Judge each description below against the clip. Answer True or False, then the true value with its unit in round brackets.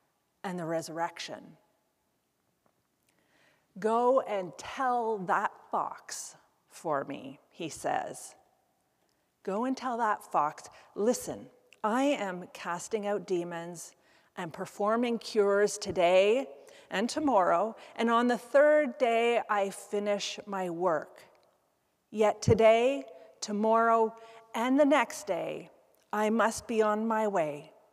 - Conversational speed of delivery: False (110 wpm)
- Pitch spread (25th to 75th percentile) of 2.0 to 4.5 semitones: True (3.9 semitones)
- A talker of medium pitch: False (215 Hz)